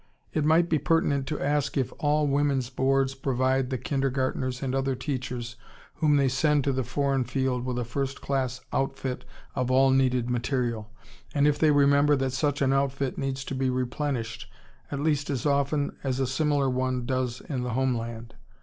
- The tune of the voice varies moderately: No, narrow, 1.9 semitones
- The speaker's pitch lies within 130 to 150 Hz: Yes, low, 135 Hz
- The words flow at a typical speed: Yes, average, 185 wpm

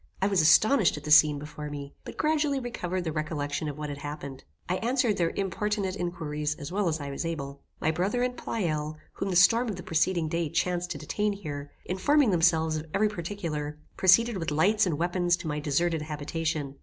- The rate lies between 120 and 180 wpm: No, fast, 205 wpm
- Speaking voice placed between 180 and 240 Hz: No, medium, 170 Hz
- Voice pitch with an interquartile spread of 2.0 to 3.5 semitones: No, average, 4.5 semitones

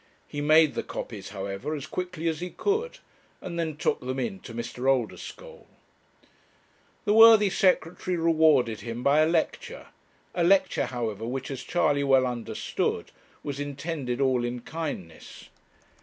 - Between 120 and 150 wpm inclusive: Yes, average, 145 wpm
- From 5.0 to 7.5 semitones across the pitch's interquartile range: Yes, wide, 5.5 semitones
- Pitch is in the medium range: Yes, medium, 145 Hz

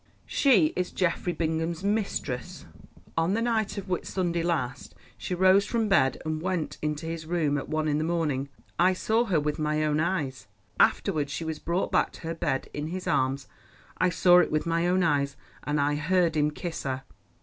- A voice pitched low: No, medium, 165 Hz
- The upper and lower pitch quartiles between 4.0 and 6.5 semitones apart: No, average, 3.4 semitones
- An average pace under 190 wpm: No, average, 195 wpm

